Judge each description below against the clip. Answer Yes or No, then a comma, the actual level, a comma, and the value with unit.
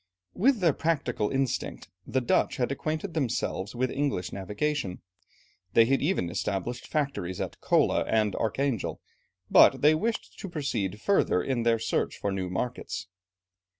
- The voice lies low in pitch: Yes, low, 125 Hz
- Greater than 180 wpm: No, average, 150 wpm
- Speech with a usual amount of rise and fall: No, wide, 6.6 semitones